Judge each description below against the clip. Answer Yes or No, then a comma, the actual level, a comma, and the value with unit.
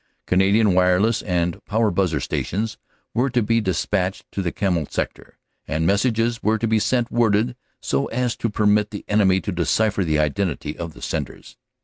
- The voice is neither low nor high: No, low, 105 Hz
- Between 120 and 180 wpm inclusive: Yes, average, 170 wpm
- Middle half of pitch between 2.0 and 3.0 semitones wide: No, average, 3.7 semitones